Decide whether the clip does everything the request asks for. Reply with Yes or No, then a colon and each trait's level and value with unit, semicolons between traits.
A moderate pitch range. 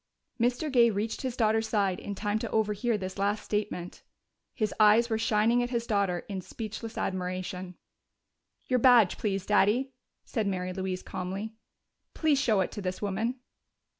Yes: average, 3.3 semitones